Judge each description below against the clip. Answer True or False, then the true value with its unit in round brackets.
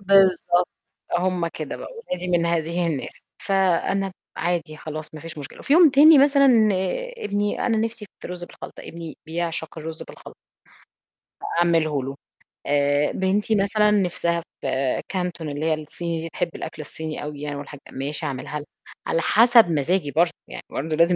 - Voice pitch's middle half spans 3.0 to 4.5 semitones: True (3.9 semitones)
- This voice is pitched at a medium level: True (170 Hz)